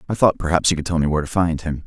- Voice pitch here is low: Yes, very low, 85 Hz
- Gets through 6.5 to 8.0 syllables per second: Yes, 7.7 syllables/s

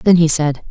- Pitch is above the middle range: No, medium, 160 Hz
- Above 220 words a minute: Yes, fast, 255 wpm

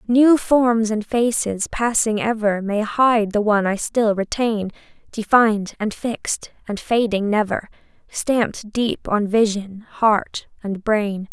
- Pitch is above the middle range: Yes, high, 215 Hz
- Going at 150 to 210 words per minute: No, average, 140 wpm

